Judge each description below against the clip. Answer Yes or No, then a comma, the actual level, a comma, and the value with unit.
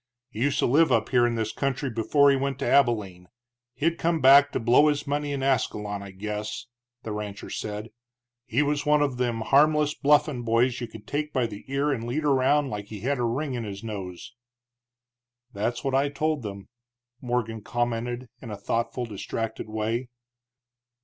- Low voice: Yes, low, 120 Hz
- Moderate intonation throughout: Yes, average, 4.4 semitones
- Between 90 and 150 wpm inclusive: No, average, 185 wpm